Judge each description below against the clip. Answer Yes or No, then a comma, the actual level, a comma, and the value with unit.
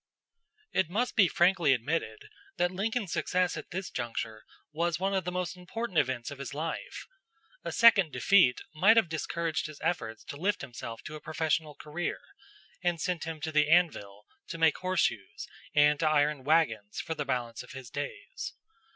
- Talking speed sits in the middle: Yes, average, 175 wpm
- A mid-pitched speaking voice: Yes, medium, 160 Hz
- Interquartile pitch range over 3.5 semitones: Yes, average, 4.3 semitones